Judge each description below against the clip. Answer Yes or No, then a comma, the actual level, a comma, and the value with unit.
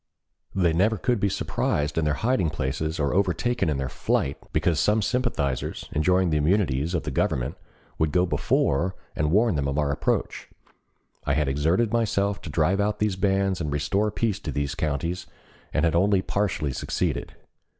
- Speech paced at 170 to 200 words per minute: Yes, average, 175 wpm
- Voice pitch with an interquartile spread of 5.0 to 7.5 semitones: Yes, average, 5.3 semitones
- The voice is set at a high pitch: No, very low, 85 Hz